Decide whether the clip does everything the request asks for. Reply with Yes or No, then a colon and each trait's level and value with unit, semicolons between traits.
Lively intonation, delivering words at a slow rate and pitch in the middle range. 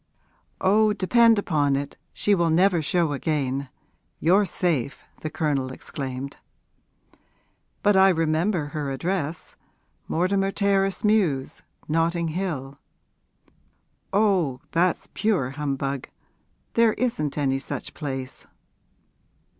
Yes: wide, 5.7 semitones; slow, 100 wpm; medium, 165 Hz